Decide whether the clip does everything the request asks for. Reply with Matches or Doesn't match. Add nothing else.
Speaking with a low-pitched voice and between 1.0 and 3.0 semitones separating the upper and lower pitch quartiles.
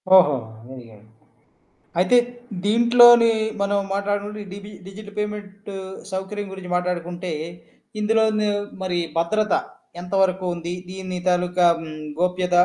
Doesn't match